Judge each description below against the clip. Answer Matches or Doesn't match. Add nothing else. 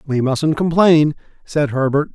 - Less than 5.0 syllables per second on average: Matches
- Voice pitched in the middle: Matches